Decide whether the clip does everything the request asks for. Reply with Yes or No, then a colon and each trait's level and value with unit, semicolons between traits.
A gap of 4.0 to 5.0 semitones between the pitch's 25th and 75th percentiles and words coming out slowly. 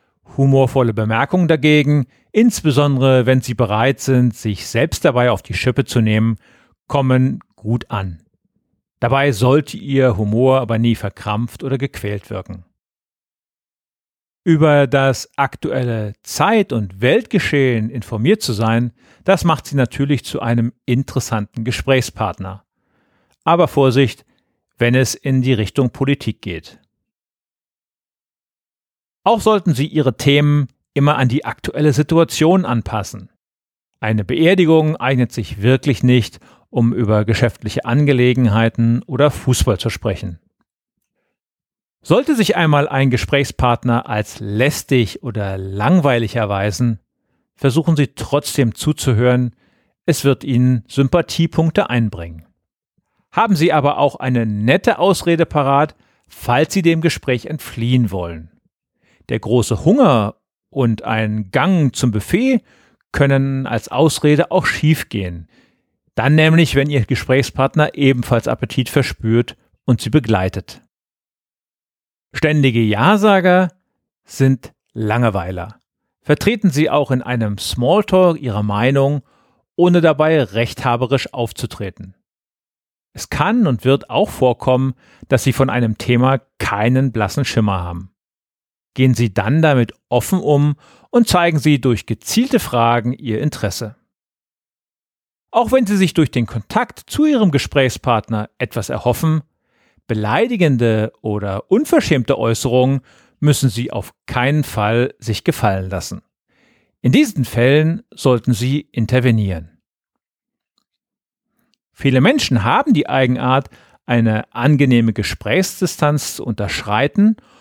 Yes: average, 4.5 semitones; slow, 115 wpm